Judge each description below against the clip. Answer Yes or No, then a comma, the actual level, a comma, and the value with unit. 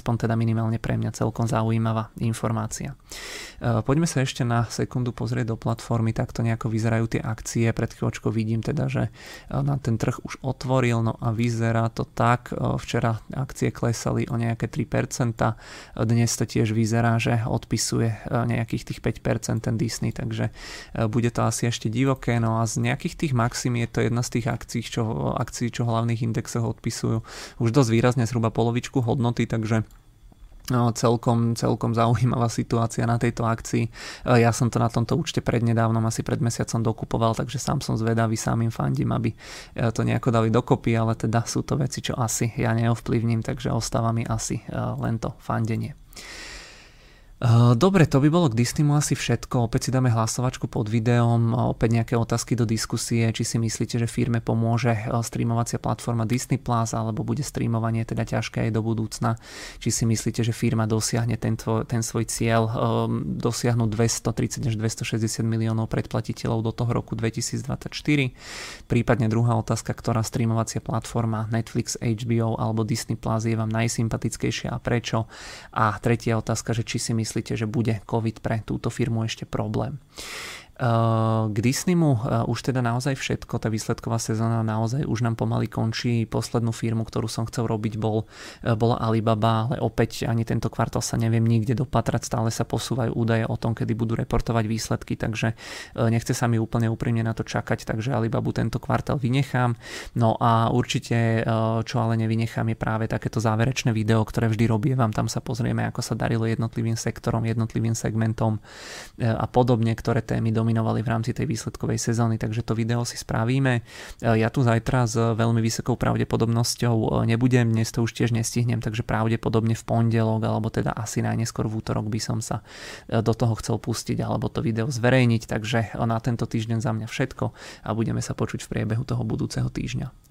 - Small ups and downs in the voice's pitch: Yes, narrow, 1.3 semitones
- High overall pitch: No, low, 115 Hz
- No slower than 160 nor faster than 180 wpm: Yes, fast, 170 wpm